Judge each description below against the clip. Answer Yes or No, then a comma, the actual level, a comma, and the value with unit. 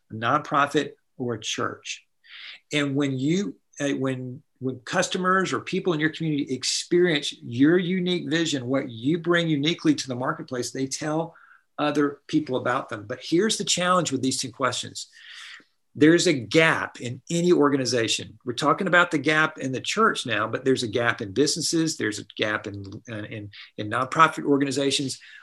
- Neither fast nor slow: Yes, average, 165 wpm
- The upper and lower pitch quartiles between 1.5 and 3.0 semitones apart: No, average, 4.3 semitones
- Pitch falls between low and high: Yes, medium, 145 Hz